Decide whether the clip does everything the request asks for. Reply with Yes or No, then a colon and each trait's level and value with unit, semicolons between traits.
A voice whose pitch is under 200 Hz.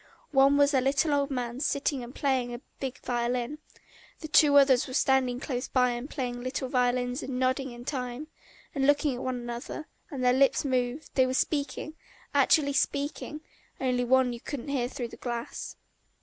No: very high, 260 Hz